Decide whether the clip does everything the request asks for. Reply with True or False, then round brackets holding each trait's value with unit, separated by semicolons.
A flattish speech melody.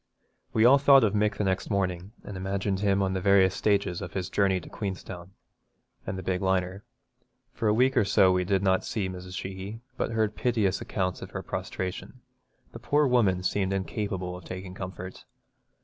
True (2.2 semitones)